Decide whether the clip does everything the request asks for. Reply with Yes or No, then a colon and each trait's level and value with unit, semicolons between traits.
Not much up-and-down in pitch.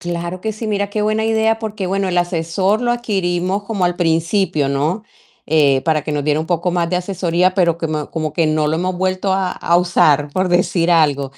No: average, 3.3 semitones